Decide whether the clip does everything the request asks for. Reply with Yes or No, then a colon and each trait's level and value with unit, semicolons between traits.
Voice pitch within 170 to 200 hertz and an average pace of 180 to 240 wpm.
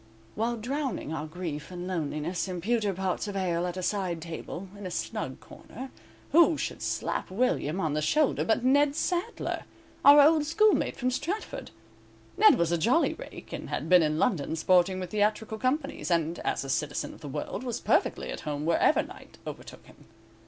Yes: high, 190 Hz; average, 185 wpm